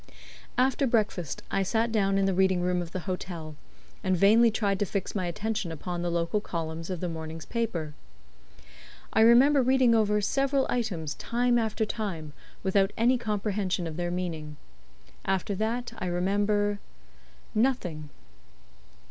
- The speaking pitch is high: Yes, high, 195 Hz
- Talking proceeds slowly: No, average, 150 wpm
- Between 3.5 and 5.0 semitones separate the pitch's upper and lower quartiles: Yes, average, 4.3 semitones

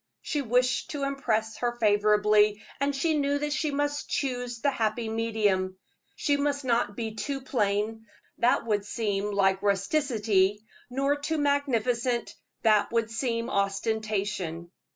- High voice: Yes, high, 230 Hz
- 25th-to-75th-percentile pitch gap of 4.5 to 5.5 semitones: Yes, average, 4.9 semitones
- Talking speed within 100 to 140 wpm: Yes, slow, 135 wpm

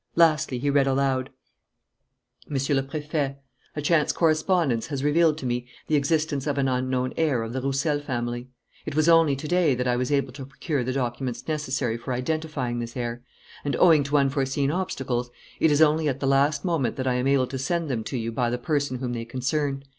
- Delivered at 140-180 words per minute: No, fast, 205 wpm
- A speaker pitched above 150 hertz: No, low, 135 Hz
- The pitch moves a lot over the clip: No, average, 3.1 semitones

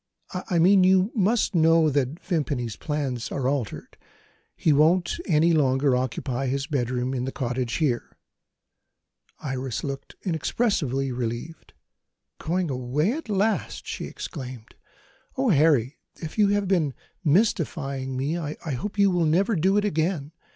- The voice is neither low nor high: Yes, medium, 150 Hz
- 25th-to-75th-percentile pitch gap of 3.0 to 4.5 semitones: No, wide, 5.5 semitones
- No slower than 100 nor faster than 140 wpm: Yes, slow, 135 wpm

